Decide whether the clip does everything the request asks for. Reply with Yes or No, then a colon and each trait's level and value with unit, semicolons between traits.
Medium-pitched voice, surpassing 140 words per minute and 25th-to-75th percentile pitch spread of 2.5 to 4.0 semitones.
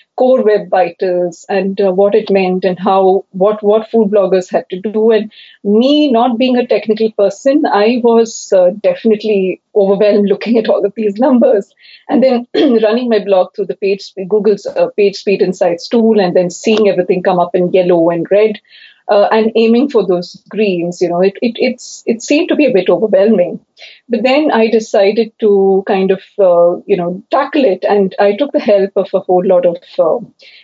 No: high, 205 Hz; average, 195 wpm; average, 3.1 semitones